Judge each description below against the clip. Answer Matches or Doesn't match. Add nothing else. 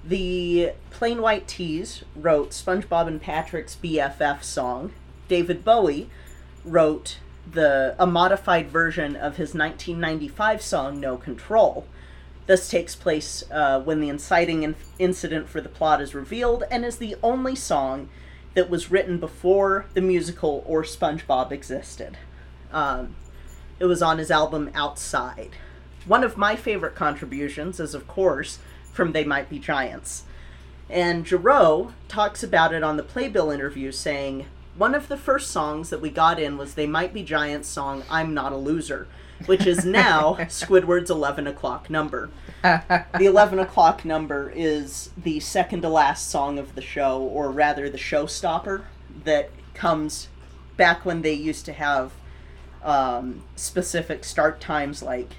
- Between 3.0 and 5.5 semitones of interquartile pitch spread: Matches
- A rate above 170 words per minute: Doesn't match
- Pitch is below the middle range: Doesn't match